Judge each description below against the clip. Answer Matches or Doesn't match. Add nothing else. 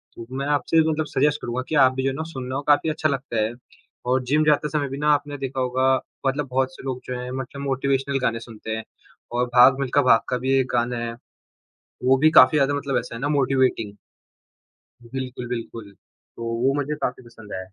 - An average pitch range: Doesn't match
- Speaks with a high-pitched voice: Doesn't match